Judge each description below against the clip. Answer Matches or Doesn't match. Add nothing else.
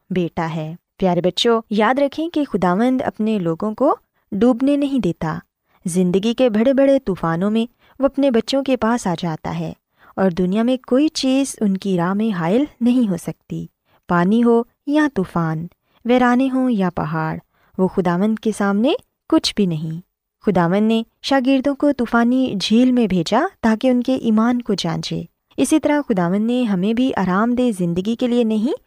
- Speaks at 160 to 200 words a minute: Matches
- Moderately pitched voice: Doesn't match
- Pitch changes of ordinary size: Doesn't match